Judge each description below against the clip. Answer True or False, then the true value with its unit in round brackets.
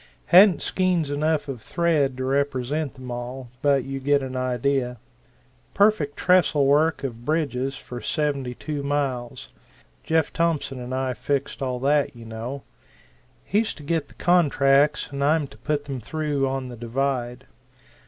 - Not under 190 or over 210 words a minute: False (155 wpm)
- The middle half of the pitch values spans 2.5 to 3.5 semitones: True (2.9 semitones)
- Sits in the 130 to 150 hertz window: True (140 Hz)